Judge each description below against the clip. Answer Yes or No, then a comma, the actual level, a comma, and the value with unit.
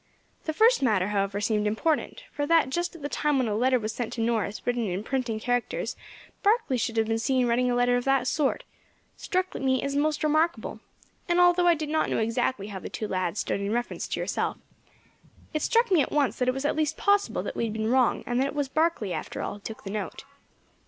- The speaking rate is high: Yes, fast, 235 wpm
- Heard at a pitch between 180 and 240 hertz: No, very high, 255 Hz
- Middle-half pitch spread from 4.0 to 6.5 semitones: Yes, wide, 5.6 semitones